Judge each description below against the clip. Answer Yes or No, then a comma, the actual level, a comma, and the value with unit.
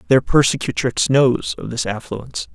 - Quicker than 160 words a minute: No, average, 140 wpm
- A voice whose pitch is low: Yes, low, 130 Hz